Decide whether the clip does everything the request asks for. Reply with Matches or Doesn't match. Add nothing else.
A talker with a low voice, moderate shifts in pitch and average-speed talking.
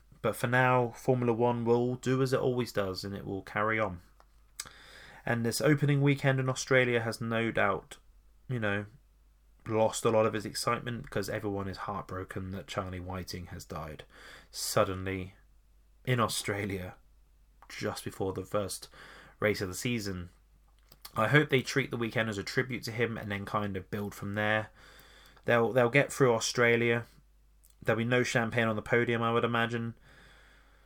Matches